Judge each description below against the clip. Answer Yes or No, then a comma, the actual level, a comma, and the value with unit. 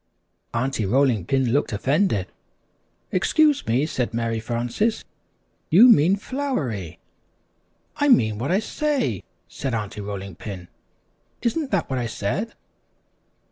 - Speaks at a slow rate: Yes, slow, 120 wpm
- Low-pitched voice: Yes, low, 130 Hz